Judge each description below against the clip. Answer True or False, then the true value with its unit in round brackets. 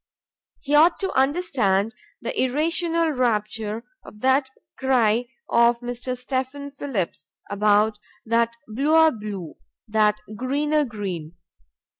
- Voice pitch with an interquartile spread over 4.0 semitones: True (5.0 semitones)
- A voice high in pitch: True (245 Hz)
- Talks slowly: True (105 wpm)